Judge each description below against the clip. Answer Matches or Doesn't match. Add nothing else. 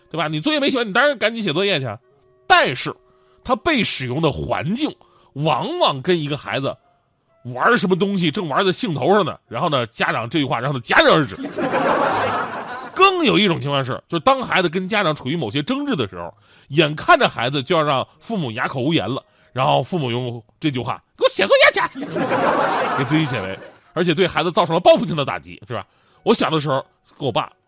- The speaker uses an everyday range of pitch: Doesn't match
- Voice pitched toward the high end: Doesn't match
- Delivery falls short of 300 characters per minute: Doesn't match